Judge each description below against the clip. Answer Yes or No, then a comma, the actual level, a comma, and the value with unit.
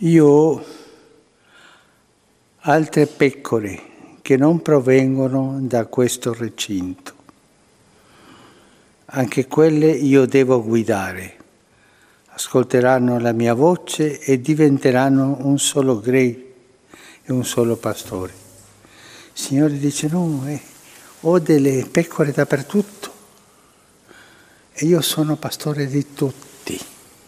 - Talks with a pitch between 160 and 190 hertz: No, low, 135 Hz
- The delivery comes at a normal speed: No, slow, 95 wpm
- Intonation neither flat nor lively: Yes, average, 3.3 semitones